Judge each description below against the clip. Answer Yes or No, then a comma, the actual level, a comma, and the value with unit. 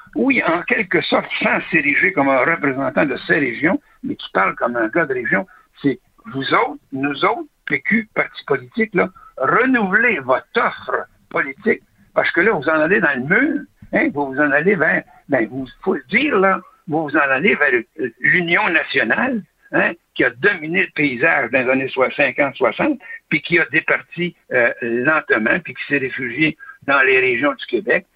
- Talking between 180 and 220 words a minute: Yes, average, 185 wpm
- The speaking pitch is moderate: Yes, medium, 170 Hz